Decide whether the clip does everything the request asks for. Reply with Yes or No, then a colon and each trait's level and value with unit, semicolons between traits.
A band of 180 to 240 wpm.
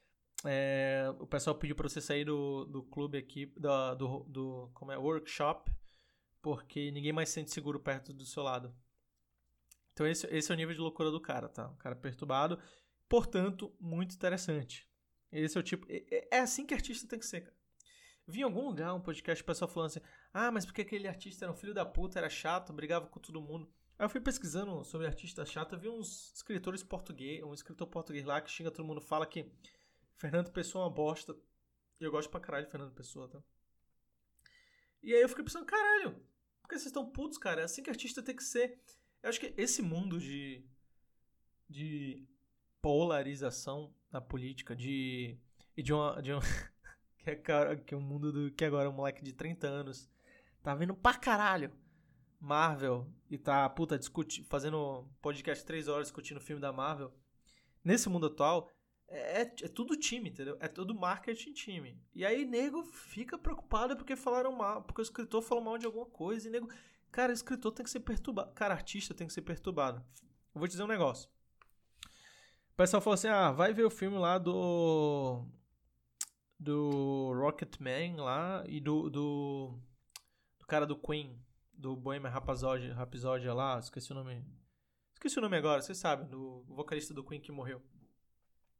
Yes: fast, 185 wpm